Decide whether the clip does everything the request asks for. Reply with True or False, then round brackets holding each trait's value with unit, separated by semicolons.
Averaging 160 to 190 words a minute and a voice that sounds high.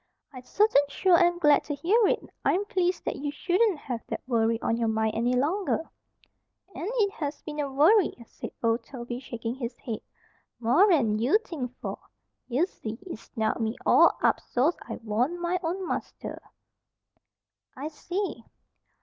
True (165 wpm; 285 Hz)